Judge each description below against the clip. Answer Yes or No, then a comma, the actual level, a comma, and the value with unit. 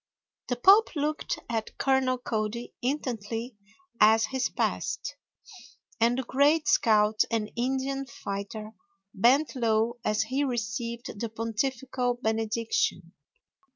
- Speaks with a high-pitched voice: Yes, high, 235 Hz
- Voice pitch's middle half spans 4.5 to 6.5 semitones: No, average, 3.1 semitones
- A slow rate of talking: Yes, slow, 110 wpm